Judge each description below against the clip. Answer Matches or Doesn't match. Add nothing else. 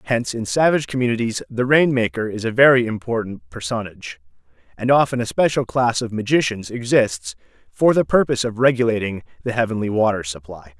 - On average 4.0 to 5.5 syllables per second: Doesn't match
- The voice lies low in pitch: Matches